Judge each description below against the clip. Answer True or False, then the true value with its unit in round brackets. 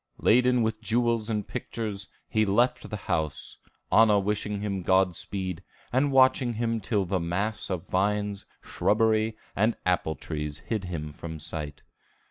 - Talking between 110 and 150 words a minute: True (140 wpm)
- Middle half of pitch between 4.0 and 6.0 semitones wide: False (3.5 semitones)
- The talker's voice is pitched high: False (105 Hz)